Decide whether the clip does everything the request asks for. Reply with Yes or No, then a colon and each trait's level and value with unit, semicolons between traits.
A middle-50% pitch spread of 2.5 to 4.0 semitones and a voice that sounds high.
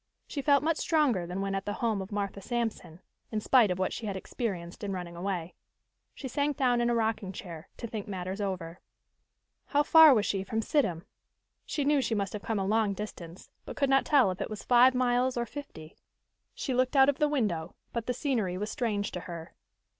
No: average, 5.3 semitones; high, 215 Hz